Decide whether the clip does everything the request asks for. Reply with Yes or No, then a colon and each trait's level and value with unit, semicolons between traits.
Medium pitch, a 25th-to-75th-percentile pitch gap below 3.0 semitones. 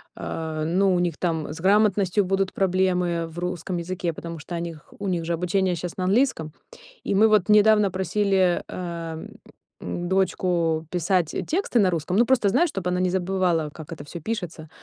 Yes: medium, 180 Hz; narrow, 2.6 semitones